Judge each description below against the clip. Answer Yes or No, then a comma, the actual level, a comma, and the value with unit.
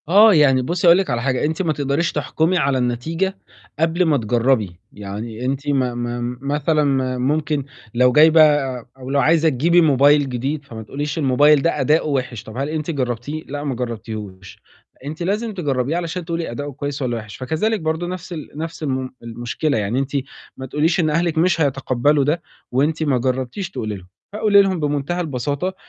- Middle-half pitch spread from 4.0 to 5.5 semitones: Yes, average, 4.3 semitones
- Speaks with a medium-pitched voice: Yes, medium, 145 Hz